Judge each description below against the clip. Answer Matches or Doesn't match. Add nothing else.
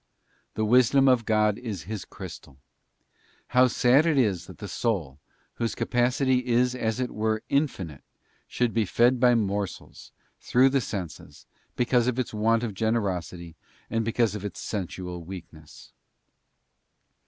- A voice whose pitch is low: Matches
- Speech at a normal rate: Matches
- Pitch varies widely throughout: Doesn't match